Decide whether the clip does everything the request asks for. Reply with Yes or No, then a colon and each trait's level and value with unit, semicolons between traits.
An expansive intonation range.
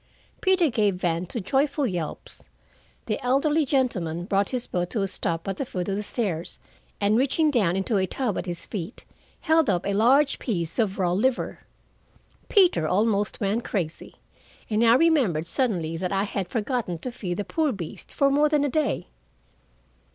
Yes: wide, 6.7 semitones